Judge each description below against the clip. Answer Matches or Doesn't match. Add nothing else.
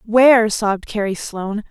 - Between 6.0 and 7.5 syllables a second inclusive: Doesn't match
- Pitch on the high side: Matches